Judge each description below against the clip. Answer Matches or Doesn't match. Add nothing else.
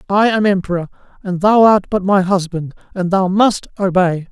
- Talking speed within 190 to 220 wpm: Doesn't match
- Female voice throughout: Doesn't match